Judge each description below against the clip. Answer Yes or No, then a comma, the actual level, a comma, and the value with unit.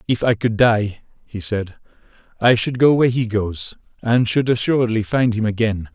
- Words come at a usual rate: Yes, average, 180 wpm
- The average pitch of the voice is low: Yes, low, 110 Hz